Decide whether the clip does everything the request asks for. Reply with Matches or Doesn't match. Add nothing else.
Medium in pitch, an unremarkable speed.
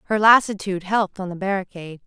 Doesn't match